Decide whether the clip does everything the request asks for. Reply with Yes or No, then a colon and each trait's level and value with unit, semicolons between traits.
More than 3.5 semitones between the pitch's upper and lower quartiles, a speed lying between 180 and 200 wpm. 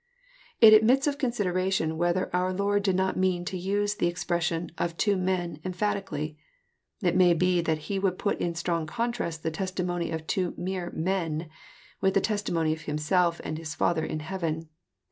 No: average, 2.7 semitones; average, 185 wpm